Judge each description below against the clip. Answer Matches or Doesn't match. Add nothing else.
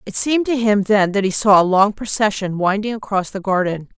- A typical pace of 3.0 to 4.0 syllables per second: Doesn't match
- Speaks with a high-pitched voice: Matches